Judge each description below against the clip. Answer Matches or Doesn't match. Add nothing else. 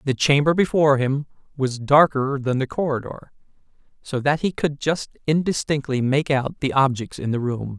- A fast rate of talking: Doesn't match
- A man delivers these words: Matches